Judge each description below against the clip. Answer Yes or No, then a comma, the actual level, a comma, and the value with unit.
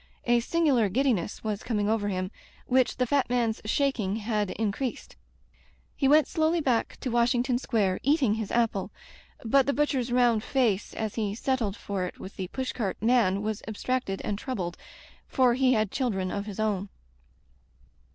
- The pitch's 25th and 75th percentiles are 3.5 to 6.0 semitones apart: Yes, average, 4.0 semitones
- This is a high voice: Yes, high, 230 Hz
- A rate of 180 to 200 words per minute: No, average, 170 wpm